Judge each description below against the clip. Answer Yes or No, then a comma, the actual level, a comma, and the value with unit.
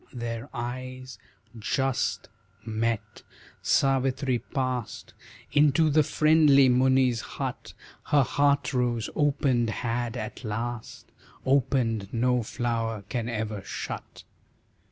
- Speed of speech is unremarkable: No, slow, 95 wpm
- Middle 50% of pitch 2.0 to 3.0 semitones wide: Yes, average, 2.7 semitones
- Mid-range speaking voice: No, low, 125 Hz